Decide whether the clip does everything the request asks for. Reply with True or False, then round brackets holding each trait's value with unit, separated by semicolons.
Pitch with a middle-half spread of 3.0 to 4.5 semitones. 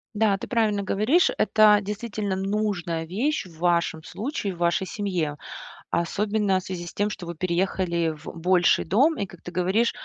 True (3.5 semitones)